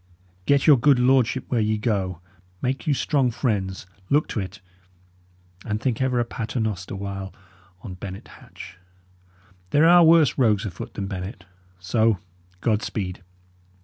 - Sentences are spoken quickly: No, average, 145 wpm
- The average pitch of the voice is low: Yes, low, 110 Hz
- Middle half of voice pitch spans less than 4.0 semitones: No, average, 5.1 semitones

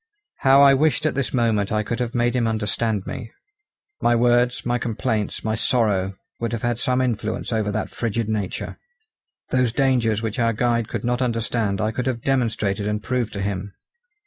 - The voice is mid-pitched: No, low, 115 Hz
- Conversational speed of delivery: Yes, average, 185 wpm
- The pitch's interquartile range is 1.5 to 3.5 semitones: Yes, narrow, 2.4 semitones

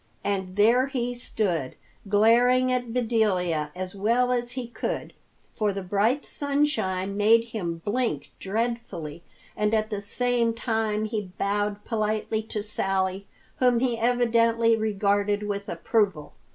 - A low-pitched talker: No, high, 215 Hz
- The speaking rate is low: Yes, slow, 130 wpm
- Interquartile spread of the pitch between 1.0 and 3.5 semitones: Yes, average, 3.0 semitones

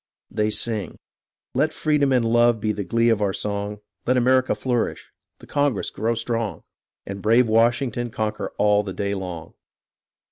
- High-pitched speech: No, low, 115 Hz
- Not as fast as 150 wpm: No, average, 165 wpm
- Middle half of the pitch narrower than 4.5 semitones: Yes, average, 2.7 semitones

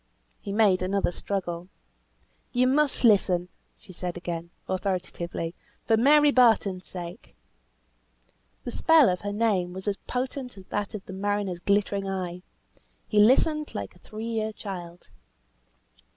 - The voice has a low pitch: No, high, 200 Hz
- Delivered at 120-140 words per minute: Yes, slow, 135 wpm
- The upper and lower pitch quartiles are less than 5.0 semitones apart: Yes, average, 3.9 semitones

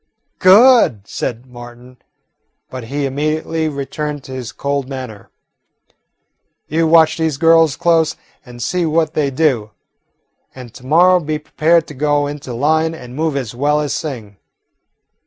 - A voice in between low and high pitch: Yes, medium, 145 Hz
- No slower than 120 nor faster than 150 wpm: Yes, average, 140 wpm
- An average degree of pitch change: Yes, average, 3.9 semitones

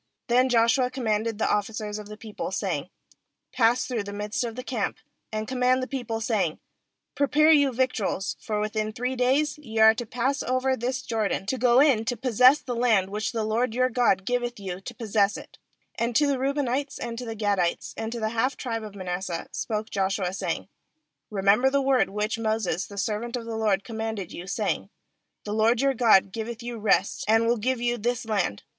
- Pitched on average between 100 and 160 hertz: No, high, 225 Hz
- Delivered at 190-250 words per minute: Yes, average, 200 wpm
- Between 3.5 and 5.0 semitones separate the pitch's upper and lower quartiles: No, average, 3.1 semitones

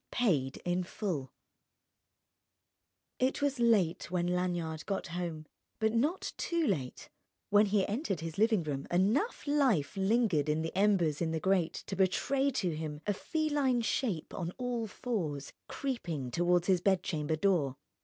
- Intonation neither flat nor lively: No, wide, 6.2 semitones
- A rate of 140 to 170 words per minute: Yes, average, 150 wpm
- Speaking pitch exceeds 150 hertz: Yes, medium, 185 Hz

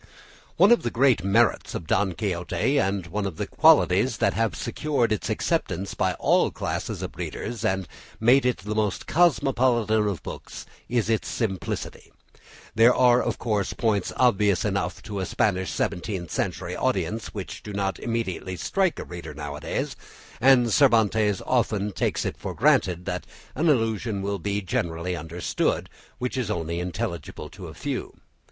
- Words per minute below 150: No, average, 165 wpm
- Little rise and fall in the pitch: No, average, 4.3 semitones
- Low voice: Yes, low, 105 Hz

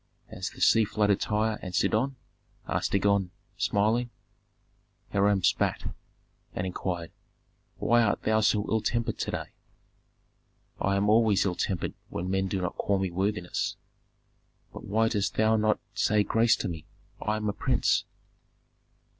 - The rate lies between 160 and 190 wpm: No, average, 145 wpm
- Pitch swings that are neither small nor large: No, narrow, 2.2 semitones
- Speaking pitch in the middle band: No, low, 105 Hz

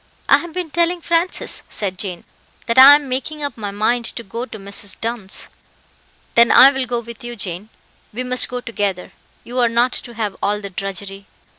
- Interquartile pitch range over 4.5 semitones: No, average, 4.1 semitones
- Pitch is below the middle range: No, high, 235 Hz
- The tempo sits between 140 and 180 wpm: No, average, 195 wpm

